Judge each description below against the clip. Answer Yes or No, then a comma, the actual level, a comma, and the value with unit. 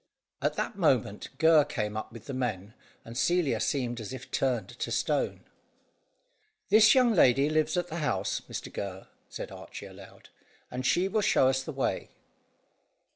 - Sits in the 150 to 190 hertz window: No, low, 130 Hz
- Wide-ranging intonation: Yes, wide, 6.0 semitones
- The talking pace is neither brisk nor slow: Yes, average, 165 wpm